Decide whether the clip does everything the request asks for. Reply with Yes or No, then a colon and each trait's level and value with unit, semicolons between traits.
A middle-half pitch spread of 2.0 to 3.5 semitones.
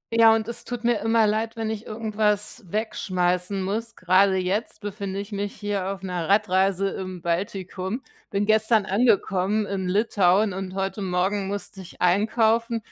Yes: narrow, 2.5 semitones